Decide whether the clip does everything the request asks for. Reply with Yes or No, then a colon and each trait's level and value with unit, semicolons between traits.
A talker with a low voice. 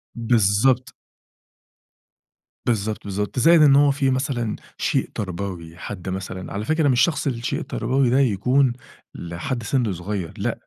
Yes: low, 120 Hz